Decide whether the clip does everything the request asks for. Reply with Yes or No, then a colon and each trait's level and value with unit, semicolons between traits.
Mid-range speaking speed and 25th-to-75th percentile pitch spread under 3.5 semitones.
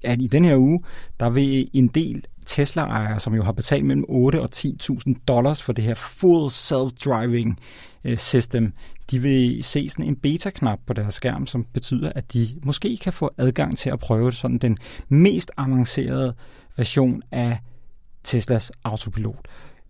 Yes: average, 160 wpm; average, 3.0 semitones